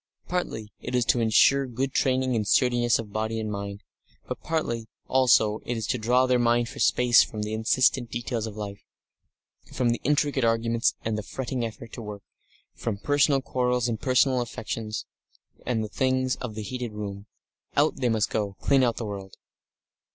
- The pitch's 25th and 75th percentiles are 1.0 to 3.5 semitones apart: Yes, average, 2.9 semitones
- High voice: No, low, 120 Hz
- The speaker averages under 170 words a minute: No, average, 190 wpm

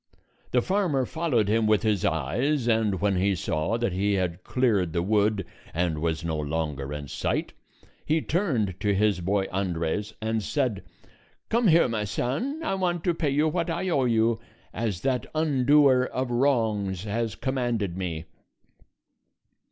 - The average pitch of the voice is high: No, low, 110 Hz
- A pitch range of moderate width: No, wide, 6.2 semitones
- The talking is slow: No, average, 160 wpm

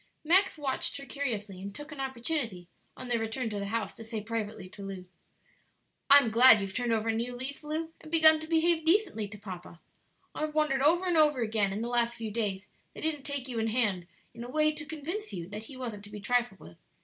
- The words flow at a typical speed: No, fast, 230 wpm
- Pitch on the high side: Yes, high, 245 Hz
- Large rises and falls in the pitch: Yes, wide, 6.1 semitones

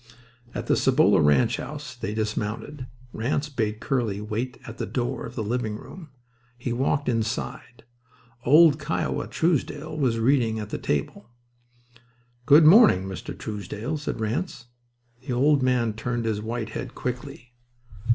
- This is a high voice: No, low, 120 Hz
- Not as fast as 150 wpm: Yes, average, 140 wpm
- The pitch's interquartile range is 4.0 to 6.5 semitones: Yes, average, 4.5 semitones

